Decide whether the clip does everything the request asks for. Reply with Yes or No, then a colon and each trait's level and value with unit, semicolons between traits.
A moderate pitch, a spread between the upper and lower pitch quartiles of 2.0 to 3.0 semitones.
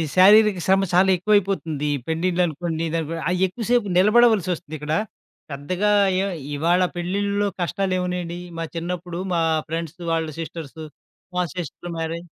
Yes: medium, 175 Hz; average, 2.7 semitones